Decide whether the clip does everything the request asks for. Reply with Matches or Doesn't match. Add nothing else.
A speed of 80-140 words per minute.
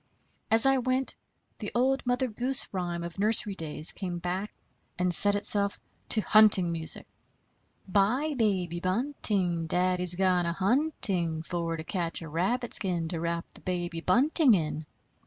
Doesn't match